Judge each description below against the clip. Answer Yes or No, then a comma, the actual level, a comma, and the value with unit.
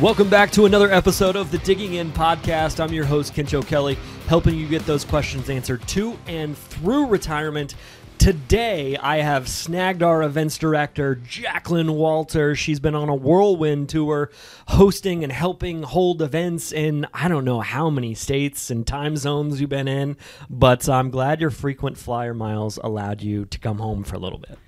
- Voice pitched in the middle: Yes, medium, 150 Hz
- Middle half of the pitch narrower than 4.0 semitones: Yes, average, 3.6 semitones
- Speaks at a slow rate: No, average, 180 wpm